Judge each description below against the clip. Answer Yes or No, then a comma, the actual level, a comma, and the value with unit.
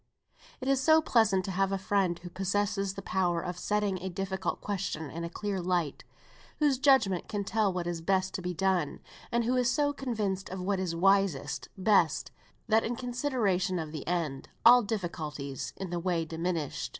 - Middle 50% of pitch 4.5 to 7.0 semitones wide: No, average, 3.5 semitones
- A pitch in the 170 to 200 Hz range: Yes, high, 190 Hz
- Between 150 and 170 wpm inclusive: No, average, 185 wpm